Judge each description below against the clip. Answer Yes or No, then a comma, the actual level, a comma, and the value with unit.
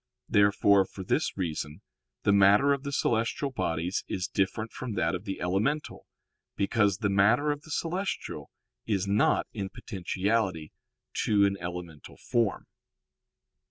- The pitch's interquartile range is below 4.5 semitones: Yes, average, 3.7 semitones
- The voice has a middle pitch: No, low, 100 Hz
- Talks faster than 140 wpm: No, slow, 135 wpm